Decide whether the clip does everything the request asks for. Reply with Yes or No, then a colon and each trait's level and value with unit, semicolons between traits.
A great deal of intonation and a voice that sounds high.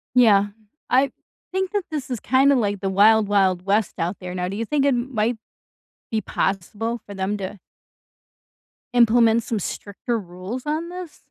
No: average, 4.4 semitones; high, 220 Hz